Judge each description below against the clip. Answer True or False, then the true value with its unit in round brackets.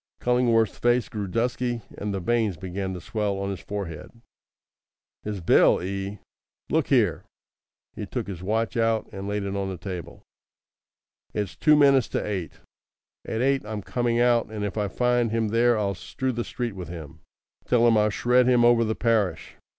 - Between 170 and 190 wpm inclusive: True (180 wpm)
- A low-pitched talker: True (110 Hz)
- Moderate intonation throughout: True (3.5 semitones)